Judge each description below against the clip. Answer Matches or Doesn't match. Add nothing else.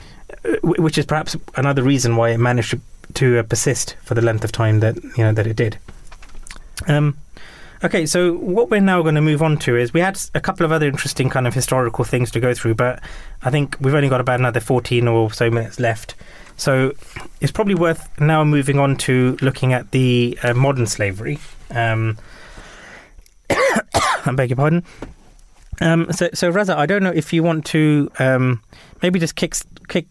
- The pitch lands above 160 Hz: Doesn't match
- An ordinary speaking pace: Matches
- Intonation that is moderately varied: Matches